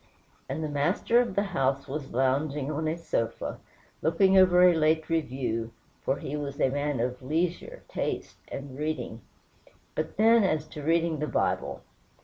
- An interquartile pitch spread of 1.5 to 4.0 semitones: Yes, average, 3.7 semitones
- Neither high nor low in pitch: Yes, medium, 155 Hz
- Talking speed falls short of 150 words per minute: No, average, 160 wpm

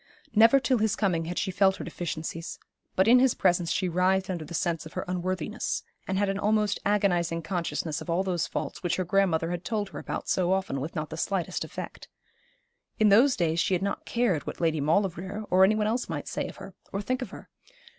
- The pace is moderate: No, fast, 225 wpm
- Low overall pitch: No, medium, 185 Hz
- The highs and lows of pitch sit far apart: No, average, 3.2 semitones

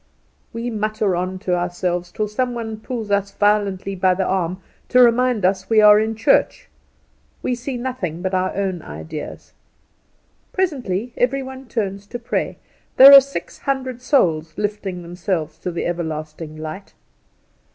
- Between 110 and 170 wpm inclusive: Yes, average, 150 wpm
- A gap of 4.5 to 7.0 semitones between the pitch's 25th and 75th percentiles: Yes, average, 5.1 semitones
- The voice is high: Yes, high, 200 Hz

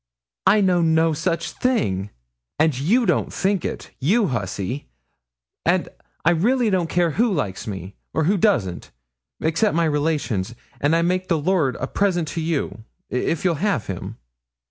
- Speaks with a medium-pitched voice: Yes, medium, 165 Hz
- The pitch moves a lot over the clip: Yes, wide, 6.1 semitones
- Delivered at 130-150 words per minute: No, average, 160 wpm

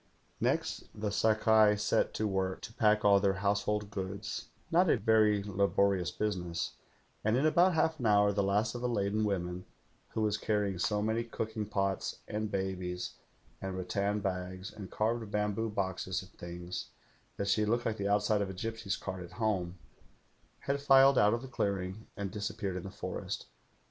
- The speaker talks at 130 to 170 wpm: No, average, 185 wpm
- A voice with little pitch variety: Yes, narrow, 2.3 semitones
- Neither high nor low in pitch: No, low, 105 Hz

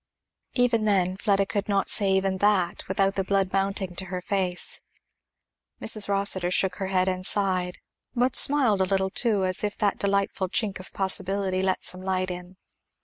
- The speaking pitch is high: Yes, high, 195 Hz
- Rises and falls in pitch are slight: Yes, narrow, 1.4 semitones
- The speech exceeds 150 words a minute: Yes, average, 175 wpm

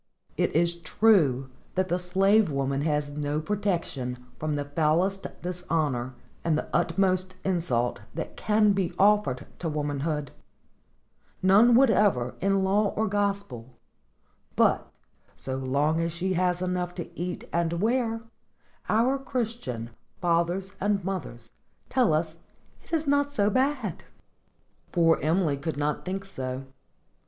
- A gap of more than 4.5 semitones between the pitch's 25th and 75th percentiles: Yes, average, 5.2 semitones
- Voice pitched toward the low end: No, medium, 175 Hz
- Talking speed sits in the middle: No, slow, 130 wpm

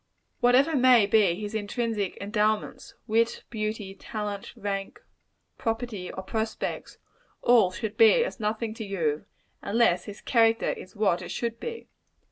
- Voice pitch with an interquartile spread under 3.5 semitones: Yes, narrow, 2.5 semitones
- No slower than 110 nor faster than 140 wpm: Yes, slow, 135 wpm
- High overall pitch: Yes, high, 215 Hz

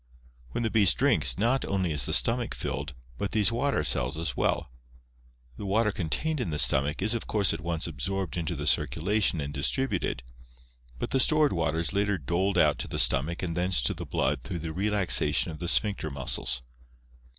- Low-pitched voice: Yes, very low, 90 Hz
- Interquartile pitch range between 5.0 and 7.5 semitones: Yes, wide, 5.4 semitones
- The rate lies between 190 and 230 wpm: Yes, average, 195 wpm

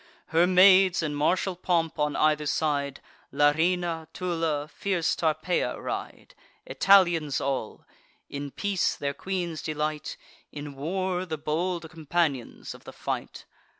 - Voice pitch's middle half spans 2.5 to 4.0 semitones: Yes, average, 3.4 semitones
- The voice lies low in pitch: No, medium, 165 Hz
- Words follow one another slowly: Yes, slow, 120 wpm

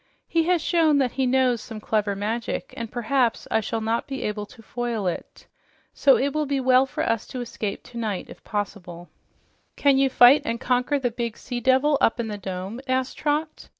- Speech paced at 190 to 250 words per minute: Yes, average, 200 wpm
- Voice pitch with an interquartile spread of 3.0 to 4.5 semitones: Yes, average, 3.5 semitones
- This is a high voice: Yes, high, 245 Hz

